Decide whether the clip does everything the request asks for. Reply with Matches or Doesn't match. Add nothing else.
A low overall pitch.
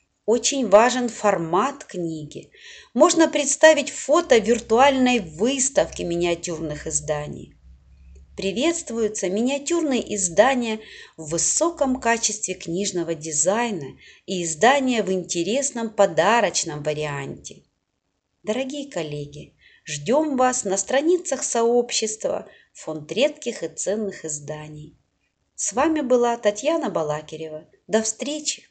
Doesn't match